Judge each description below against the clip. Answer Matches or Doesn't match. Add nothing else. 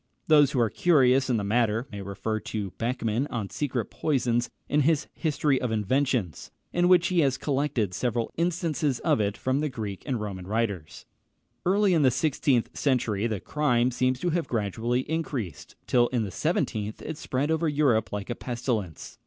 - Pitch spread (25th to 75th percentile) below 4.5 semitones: Doesn't match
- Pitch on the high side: Doesn't match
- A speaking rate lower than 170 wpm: Doesn't match